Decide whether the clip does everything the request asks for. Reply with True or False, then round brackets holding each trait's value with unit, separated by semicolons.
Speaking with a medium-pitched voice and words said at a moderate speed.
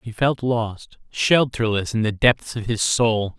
False (115 Hz; 175 wpm)